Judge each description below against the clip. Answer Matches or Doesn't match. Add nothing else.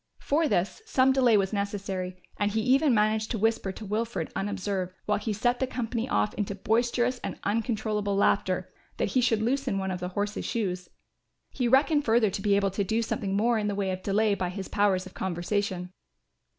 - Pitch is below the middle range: Doesn't match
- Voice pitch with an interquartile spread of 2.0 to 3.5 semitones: Matches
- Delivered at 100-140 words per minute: Doesn't match